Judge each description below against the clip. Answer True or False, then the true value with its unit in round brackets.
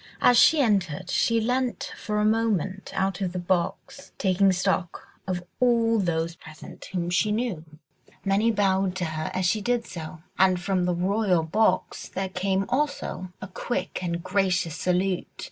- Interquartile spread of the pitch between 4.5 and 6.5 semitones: False (3.1 semitones)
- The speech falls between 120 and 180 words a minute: True (160 wpm)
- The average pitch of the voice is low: False (190 Hz)